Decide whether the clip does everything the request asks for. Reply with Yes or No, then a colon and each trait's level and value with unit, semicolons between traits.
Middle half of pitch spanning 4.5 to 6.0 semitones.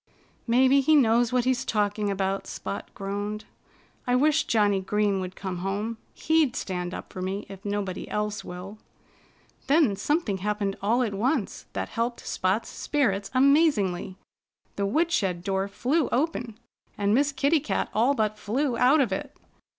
Yes: average, 4.8 semitones